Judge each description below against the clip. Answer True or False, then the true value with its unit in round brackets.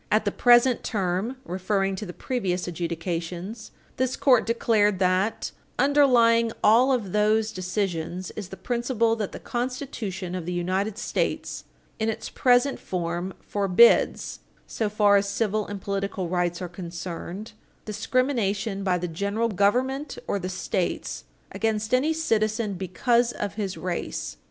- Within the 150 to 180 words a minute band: False (140 wpm)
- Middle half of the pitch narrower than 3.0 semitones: False (4.0 semitones)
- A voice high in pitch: True (205 Hz)